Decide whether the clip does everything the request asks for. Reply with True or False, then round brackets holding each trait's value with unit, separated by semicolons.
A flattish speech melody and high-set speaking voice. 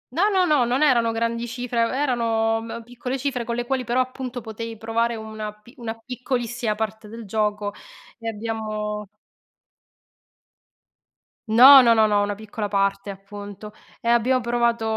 True (2.1 semitones; 230 Hz)